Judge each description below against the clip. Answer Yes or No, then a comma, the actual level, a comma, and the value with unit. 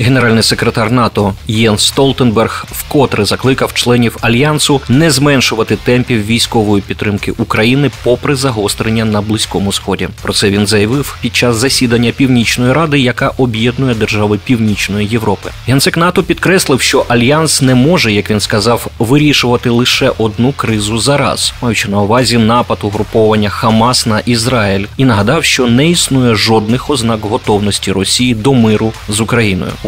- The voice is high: No, low, 115 Hz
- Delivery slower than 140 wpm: No, average, 145 wpm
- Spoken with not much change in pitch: No, average, 3.4 semitones